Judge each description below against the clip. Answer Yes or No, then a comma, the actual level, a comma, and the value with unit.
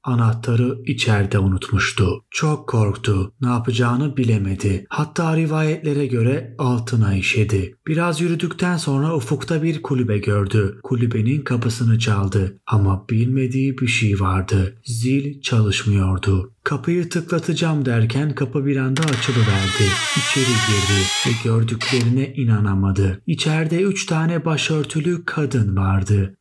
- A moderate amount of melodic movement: No, wide, 6.0 semitones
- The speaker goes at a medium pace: Yes, average, 110 wpm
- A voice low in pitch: Yes, low, 125 Hz